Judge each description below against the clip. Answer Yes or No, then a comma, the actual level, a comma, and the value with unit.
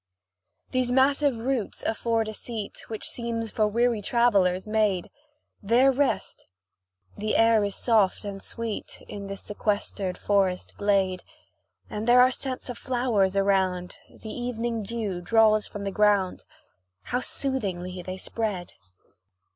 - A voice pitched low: No, high, 215 Hz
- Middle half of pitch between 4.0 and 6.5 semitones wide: No, average, 3.3 semitones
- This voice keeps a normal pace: No, slow, 130 wpm